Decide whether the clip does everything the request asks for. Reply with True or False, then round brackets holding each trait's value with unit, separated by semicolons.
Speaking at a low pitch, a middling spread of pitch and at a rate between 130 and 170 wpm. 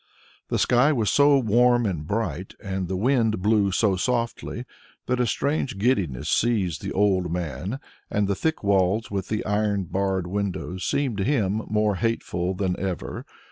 True (105 Hz; 3.7 semitones; 165 wpm)